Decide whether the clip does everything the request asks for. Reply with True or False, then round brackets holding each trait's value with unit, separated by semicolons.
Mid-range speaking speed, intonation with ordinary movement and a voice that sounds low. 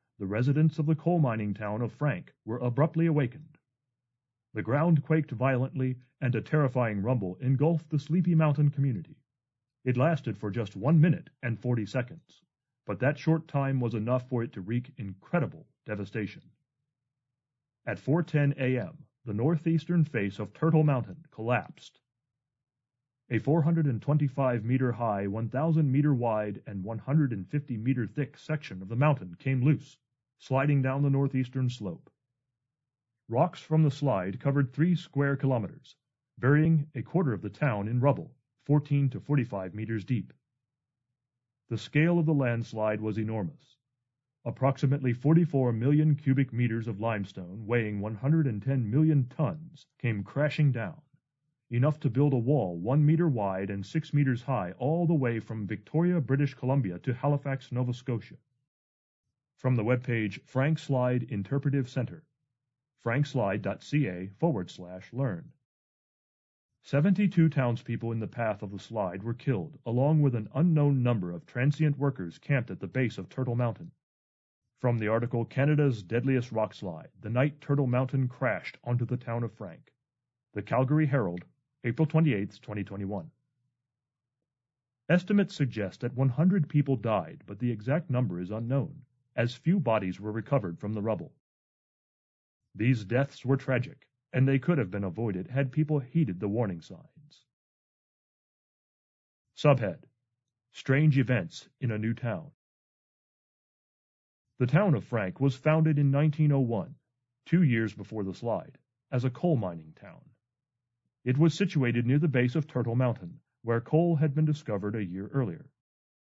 True (145 wpm; 4.0 semitones; 130 Hz)